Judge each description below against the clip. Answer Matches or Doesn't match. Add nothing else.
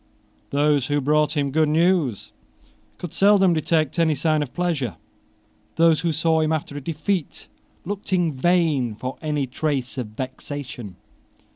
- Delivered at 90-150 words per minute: Matches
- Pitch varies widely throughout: Doesn't match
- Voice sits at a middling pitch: Matches